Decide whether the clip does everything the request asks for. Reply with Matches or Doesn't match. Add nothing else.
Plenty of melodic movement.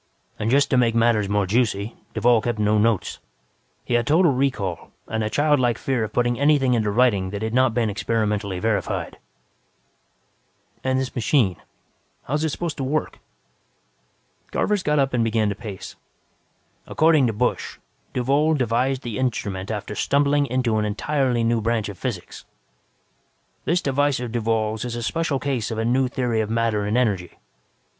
Doesn't match